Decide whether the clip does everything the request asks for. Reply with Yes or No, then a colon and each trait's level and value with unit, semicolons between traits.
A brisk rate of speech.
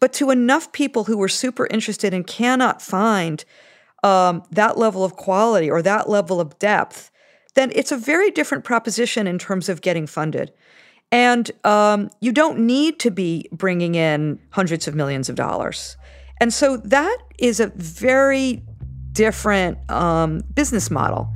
No: average, 155 wpm